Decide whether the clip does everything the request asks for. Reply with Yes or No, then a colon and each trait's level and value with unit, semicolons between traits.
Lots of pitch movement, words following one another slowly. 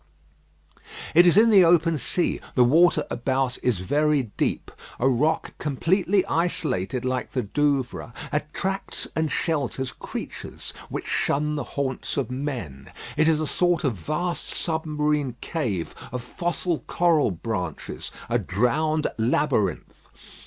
No: average, 4.5 semitones; slow, 130 wpm